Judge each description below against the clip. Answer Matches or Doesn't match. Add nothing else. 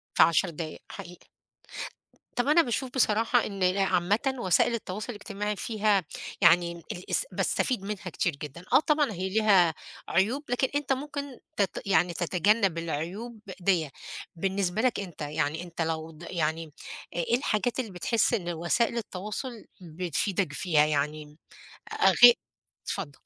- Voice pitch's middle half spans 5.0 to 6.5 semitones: Matches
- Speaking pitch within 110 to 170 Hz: Doesn't match